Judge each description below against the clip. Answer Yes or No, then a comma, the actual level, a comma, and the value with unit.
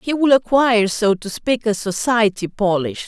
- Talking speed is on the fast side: No, average, 175 wpm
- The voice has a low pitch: No, high, 220 Hz